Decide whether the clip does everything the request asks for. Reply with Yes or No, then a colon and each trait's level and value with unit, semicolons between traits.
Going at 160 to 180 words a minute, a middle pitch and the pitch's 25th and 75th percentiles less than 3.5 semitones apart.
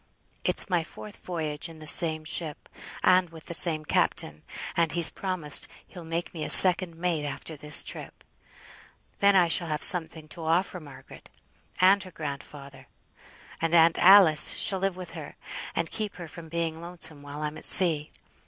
Yes: average, 170 wpm; medium, 165 Hz; average, 2.7 semitones